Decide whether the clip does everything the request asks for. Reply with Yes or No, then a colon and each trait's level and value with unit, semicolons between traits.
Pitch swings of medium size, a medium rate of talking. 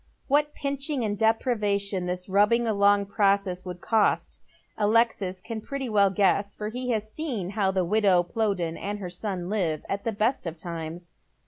Yes: average, 3.4 semitones; average, 165 wpm